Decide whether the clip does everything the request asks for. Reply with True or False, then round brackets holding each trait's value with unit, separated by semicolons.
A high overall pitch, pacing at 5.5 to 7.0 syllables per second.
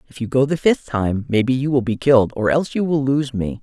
False (130 Hz; 5.9 syllables/s)